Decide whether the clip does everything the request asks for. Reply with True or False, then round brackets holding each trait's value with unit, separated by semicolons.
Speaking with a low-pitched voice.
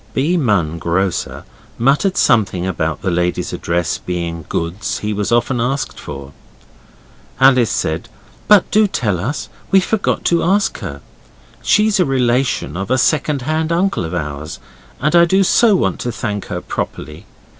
True (115 Hz)